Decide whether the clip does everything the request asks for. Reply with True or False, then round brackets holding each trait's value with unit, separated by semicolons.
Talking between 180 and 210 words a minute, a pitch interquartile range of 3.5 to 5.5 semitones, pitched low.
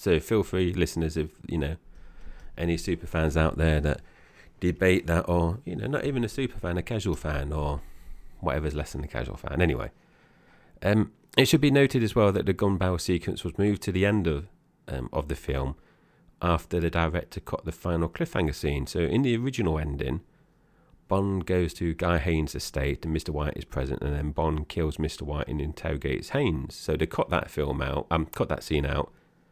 True (205 wpm; 3.8 semitones; 85 Hz)